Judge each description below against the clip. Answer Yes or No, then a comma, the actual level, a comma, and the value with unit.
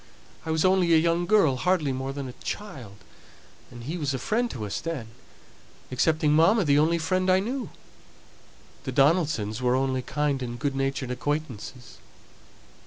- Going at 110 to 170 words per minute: Yes, average, 165 wpm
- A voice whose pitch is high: No, medium, 150 Hz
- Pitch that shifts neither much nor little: Yes, average, 4.7 semitones